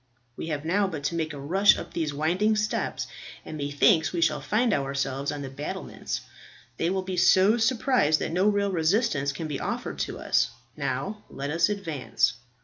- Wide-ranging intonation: Yes, wide, 5.8 semitones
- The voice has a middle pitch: Yes, medium, 165 Hz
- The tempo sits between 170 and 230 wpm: Yes, average, 185 wpm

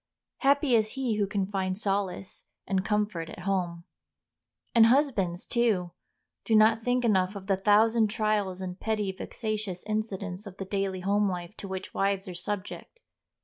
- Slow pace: No, average, 160 wpm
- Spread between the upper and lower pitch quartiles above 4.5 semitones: No, narrow, 2.5 semitones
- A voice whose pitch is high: Yes, high, 200 Hz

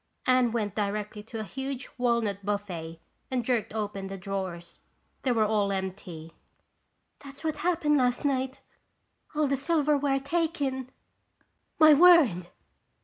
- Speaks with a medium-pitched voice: No, high, 240 Hz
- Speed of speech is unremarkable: No, slow, 130 wpm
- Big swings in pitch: Yes, wide, 5.7 semitones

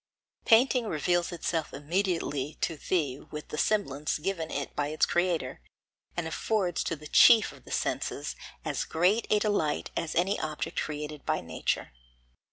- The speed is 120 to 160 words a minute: Yes, average, 155 wpm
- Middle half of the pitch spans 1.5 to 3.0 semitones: No, average, 4.1 semitones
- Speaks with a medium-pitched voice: Yes, medium, 160 Hz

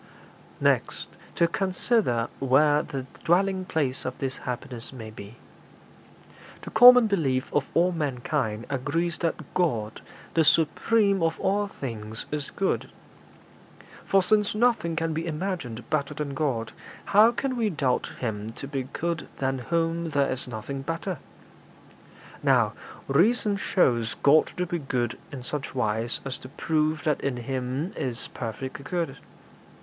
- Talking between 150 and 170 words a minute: No, average, 140 wpm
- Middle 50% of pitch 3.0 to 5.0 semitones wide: No, wide, 5.4 semitones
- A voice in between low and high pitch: Yes, medium, 145 Hz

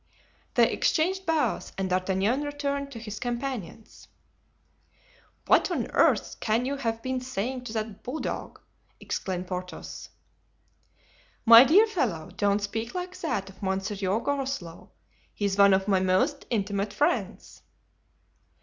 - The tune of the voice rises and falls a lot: Yes, wide, 6.0 semitones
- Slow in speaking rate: Yes, slow, 125 wpm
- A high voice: Yes, high, 225 Hz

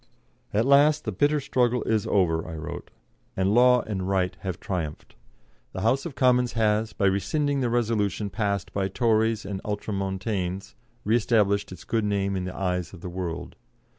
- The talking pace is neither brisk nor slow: Yes, average, 170 wpm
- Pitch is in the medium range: No, low, 105 Hz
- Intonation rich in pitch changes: No, average, 3.8 semitones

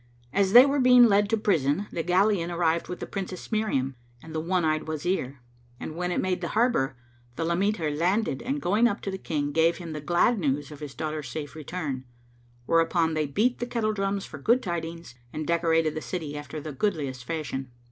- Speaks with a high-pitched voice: No, medium, 170 Hz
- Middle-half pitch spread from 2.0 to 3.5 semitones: No, average, 4.5 semitones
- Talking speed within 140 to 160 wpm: No, average, 200 wpm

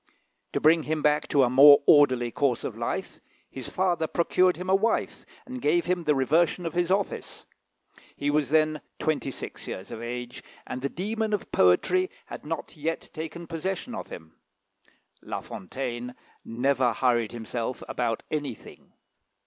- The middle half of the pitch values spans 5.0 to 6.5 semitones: Yes, wide, 5.6 semitones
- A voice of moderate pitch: Yes, medium, 150 Hz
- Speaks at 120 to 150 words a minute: No, average, 160 wpm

